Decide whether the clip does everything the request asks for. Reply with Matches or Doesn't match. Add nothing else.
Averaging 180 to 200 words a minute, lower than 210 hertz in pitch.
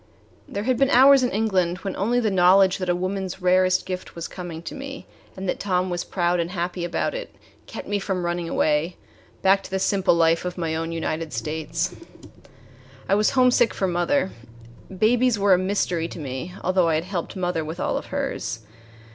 Matches